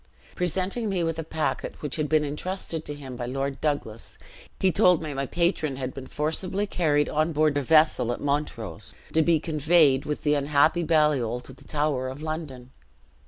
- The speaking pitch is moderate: Yes, medium, 150 Hz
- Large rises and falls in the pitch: No, average, 3.0 semitones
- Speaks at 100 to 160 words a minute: No, average, 185 wpm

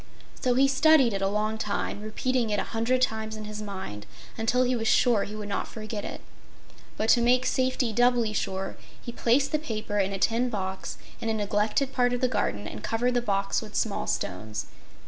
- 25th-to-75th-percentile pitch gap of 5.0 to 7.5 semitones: No, average, 3.3 semitones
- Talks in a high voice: Yes, high, 220 Hz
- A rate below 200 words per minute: No, fast, 205 wpm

